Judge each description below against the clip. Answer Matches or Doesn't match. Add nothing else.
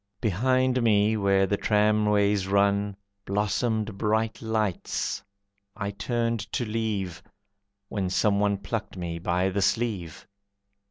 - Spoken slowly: Matches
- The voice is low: Matches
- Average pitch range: Doesn't match